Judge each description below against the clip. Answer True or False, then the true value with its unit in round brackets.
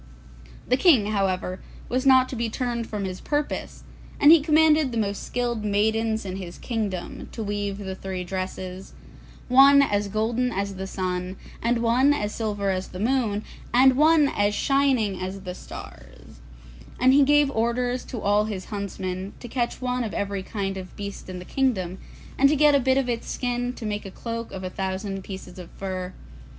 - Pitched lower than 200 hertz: False (215 Hz)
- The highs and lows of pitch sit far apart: False (4.7 semitones)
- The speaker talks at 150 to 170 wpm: False (185 wpm)